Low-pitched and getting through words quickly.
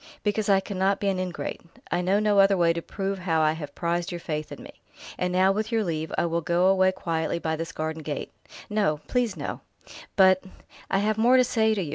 No: medium, 185 Hz; fast, 240 wpm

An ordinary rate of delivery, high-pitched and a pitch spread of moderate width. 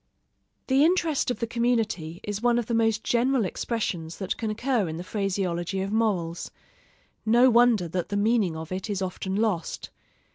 Yes: average, 175 wpm; high, 215 Hz; average, 4.3 semitones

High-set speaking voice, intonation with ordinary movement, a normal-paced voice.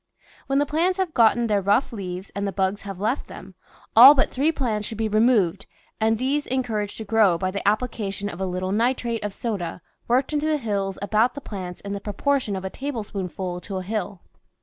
No: high, 215 Hz; average, 4.3 semitones; fast, 215 wpm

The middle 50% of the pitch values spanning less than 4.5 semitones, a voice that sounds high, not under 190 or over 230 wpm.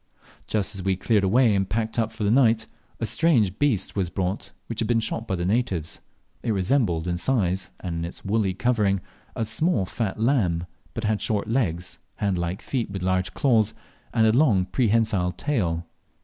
No: average, 3.8 semitones; low, 105 Hz; average, 195 wpm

